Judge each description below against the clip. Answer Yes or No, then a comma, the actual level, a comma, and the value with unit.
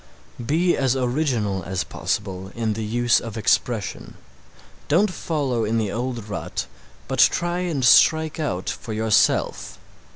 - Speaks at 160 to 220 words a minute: No, slow, 135 wpm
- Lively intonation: Yes, wide, 5.8 semitones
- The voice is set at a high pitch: No, low, 120 Hz